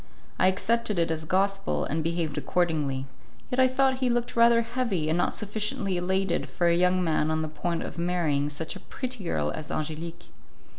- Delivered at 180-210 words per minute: Yes, average, 190 wpm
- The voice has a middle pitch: Yes, medium, 175 Hz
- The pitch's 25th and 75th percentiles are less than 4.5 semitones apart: No, average, 4.9 semitones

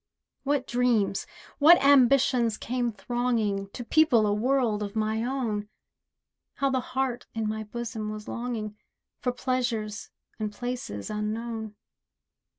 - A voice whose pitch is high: Yes, high, 235 Hz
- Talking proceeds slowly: Yes, slow, 125 wpm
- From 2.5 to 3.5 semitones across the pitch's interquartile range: Yes, average, 2.9 semitones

